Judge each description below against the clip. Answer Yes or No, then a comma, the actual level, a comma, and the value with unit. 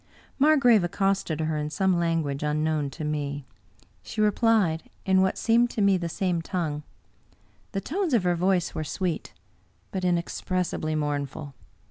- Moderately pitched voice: Yes, medium, 175 Hz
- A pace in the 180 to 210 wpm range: No, average, 150 wpm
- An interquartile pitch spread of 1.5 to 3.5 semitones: No, average, 4.2 semitones